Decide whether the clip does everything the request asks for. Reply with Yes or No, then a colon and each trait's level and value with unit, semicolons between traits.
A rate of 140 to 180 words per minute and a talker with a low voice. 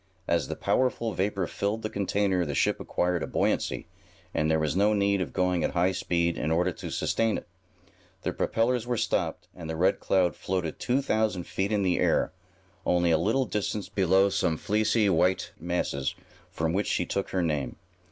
No: average, 190 wpm; very low, 95 Hz